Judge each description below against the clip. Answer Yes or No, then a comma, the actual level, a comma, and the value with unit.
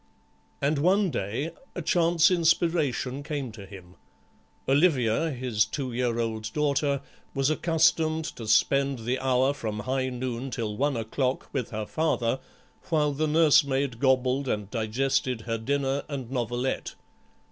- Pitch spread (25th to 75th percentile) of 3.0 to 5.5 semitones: Yes, average, 4.1 semitones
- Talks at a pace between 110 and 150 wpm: Yes, slow, 135 wpm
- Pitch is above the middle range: No, low, 135 Hz